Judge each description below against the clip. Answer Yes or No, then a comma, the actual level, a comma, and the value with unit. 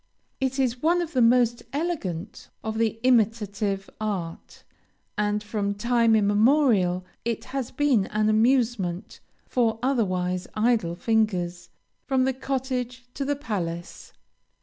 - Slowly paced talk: Yes, slow, 125 wpm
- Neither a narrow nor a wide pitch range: Yes, average, 4.1 semitones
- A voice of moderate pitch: No, high, 225 Hz